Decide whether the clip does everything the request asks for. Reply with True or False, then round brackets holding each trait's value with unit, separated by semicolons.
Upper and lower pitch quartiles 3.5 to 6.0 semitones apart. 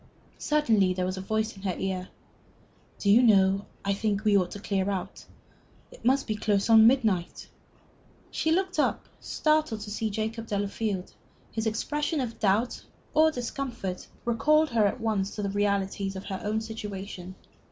False (3.0 semitones)